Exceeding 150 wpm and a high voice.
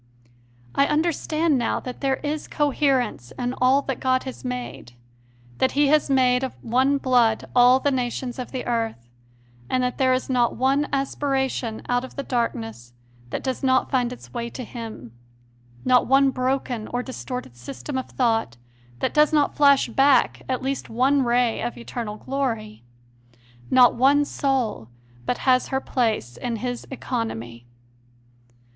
Yes: average, 160 wpm; very high, 255 Hz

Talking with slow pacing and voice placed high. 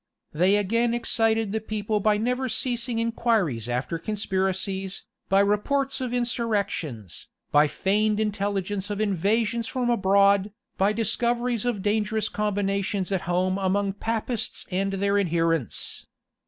Yes: slow, 125 wpm; high, 205 Hz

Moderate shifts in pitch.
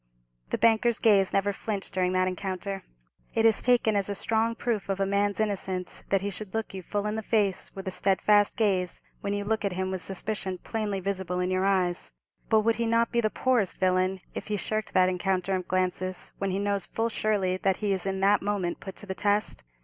No: narrow, 2.3 semitones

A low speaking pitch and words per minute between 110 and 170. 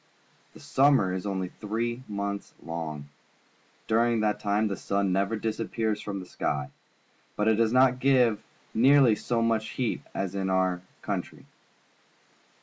Yes: low, 105 Hz; average, 145 wpm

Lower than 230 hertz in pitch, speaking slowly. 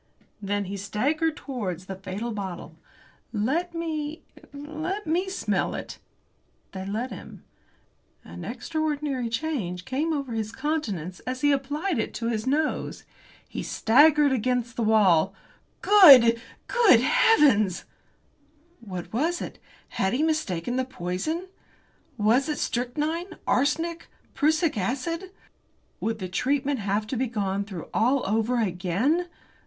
No: very high, 255 Hz; slow, 125 wpm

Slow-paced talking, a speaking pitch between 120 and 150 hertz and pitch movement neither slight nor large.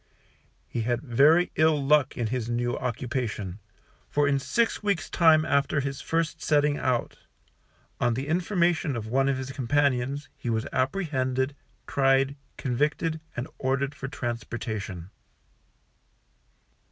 Yes: slow, 130 wpm; low, 135 Hz; average, 3.6 semitones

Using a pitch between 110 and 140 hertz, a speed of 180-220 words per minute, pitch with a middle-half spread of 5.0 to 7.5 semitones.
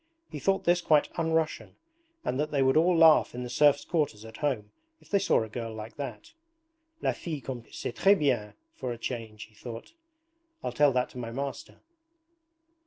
Yes: low, 135 Hz; average, 195 wpm; average, 5.3 semitones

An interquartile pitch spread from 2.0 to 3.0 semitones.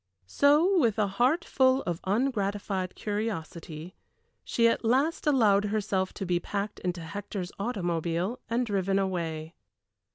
No: average, 4.6 semitones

